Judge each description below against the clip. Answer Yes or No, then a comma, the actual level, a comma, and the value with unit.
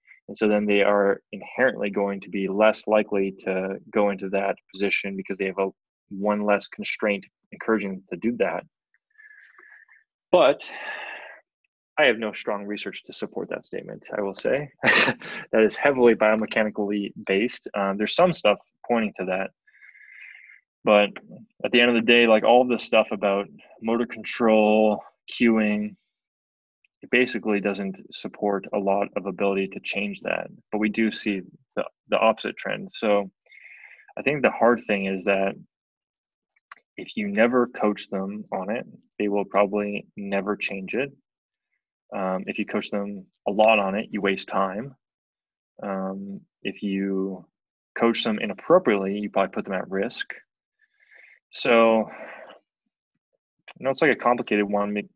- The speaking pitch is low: Yes, low, 105 Hz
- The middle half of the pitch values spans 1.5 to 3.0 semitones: Yes, narrow, 2.6 semitones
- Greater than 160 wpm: No, average, 155 wpm